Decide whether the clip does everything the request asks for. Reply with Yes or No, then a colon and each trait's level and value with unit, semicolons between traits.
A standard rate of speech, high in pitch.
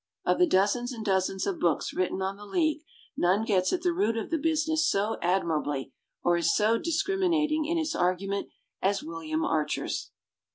Yes: average, 180 wpm; high, 205 Hz